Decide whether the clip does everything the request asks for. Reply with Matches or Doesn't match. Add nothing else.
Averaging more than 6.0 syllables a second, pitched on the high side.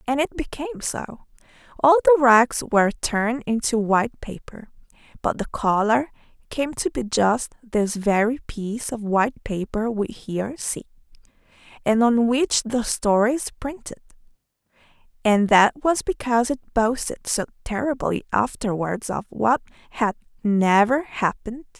Doesn't match